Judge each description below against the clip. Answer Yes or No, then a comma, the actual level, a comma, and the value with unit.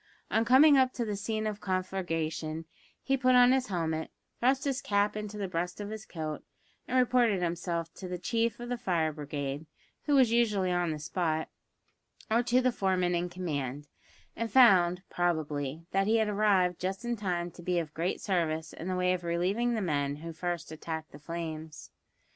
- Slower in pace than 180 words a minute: No, average, 190 wpm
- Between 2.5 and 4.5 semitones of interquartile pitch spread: No, average, 5.1 semitones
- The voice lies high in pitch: No, medium, 180 Hz